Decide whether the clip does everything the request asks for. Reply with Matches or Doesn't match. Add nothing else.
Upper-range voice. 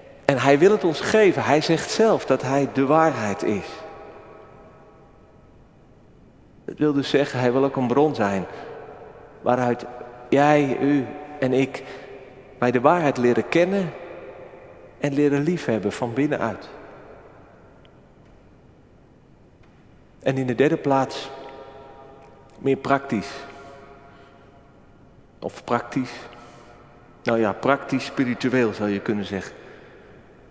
Doesn't match